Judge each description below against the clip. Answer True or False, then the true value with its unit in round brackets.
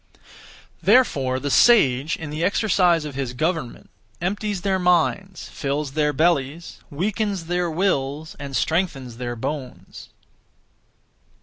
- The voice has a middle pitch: True (160 Hz)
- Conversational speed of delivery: False (115 wpm)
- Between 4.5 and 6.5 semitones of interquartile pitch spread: True (5.2 semitones)